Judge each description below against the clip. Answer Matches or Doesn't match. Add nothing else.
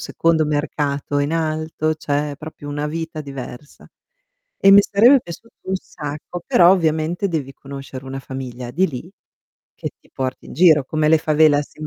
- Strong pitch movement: Doesn't match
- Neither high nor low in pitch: Matches